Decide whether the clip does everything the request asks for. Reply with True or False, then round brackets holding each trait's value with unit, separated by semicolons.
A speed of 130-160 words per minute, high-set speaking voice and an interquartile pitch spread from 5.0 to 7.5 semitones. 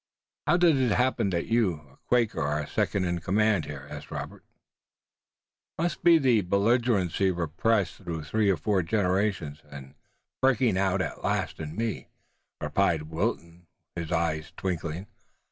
False (145 wpm; 95 Hz; 5.3 semitones)